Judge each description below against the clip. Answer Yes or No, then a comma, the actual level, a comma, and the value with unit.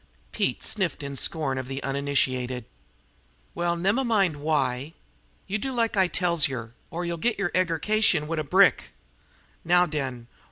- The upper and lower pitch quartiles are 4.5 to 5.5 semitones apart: Yes, average, 5.2 semitones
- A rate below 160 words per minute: Yes, average, 150 wpm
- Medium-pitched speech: Yes, medium, 160 Hz